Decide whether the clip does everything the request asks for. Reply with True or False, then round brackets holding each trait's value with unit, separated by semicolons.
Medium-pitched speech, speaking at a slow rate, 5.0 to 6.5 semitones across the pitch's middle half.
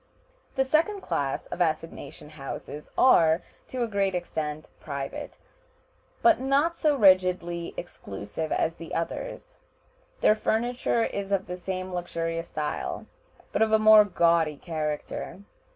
True (180 Hz; 130 wpm; 5.6 semitones)